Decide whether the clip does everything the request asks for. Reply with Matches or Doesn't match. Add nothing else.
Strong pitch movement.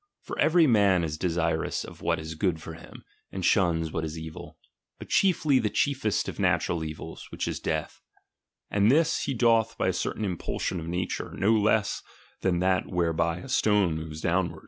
Doesn't match